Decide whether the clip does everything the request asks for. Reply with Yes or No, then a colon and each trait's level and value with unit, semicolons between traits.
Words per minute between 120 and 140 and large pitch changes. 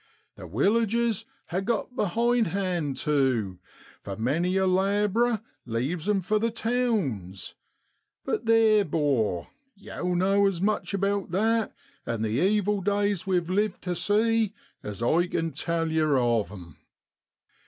Yes: slow, 135 wpm; wide, 6.6 semitones